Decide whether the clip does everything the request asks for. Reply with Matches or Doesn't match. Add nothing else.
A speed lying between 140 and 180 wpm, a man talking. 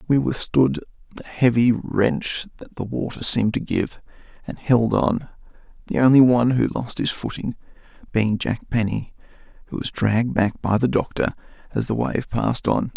Matches